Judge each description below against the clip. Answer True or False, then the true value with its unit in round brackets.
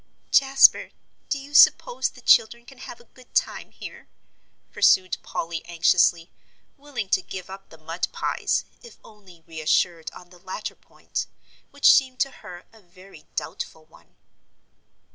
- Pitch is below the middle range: False (190 Hz)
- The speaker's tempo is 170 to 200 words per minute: False (145 wpm)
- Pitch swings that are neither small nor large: False (7.0 semitones)